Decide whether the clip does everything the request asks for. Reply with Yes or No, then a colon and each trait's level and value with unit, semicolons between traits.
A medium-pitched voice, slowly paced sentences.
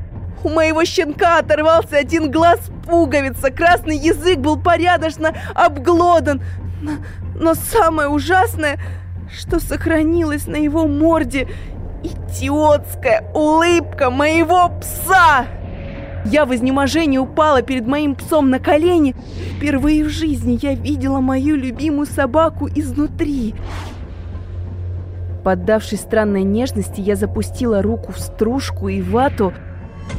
No: very high, 285 Hz; slow, 105 wpm